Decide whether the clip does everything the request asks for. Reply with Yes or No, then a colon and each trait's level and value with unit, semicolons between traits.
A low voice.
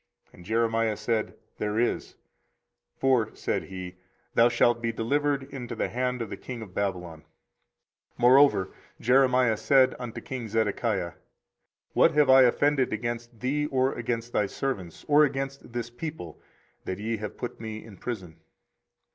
Yes: low, 120 Hz